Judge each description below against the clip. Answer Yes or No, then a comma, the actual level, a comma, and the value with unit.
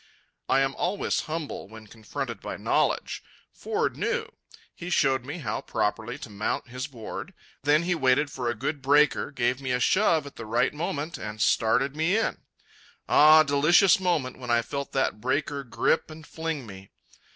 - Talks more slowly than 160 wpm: No, average, 175 wpm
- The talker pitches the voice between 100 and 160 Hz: Yes, medium, 140 Hz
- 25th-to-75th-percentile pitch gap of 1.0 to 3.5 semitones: No, average, 4.6 semitones